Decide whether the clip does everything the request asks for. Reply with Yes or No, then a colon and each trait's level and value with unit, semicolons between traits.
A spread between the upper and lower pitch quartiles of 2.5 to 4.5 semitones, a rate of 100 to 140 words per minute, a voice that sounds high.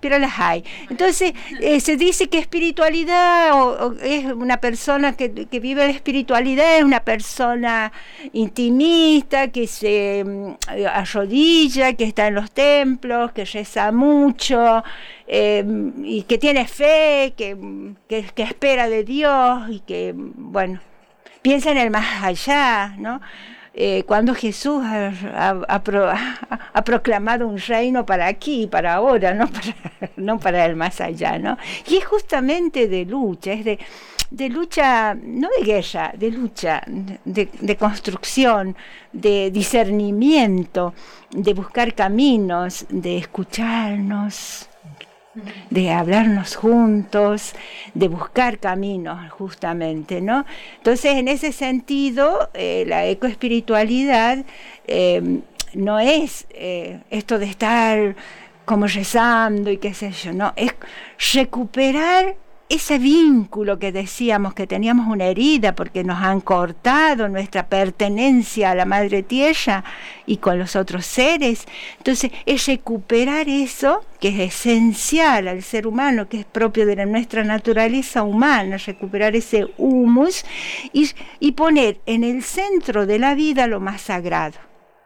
No: average, 5.1 semitones; average, 130 wpm; high, 225 Hz